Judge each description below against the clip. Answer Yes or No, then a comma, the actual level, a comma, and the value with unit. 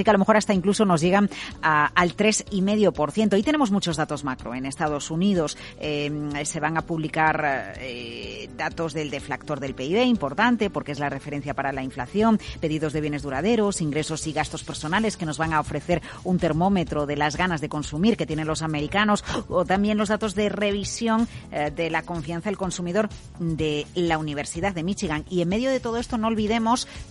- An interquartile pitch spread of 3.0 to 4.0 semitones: No, average, 5.3 semitones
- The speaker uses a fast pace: Yes, fast, 200 wpm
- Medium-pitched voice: Yes, medium, 165 Hz